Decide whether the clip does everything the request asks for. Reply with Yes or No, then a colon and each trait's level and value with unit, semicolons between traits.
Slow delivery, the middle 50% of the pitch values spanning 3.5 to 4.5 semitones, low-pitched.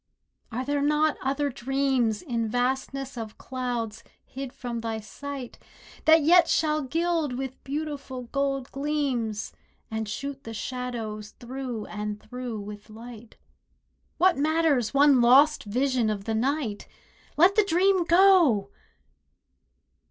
No: slow, 125 wpm; average, 4.2 semitones; very high, 260 Hz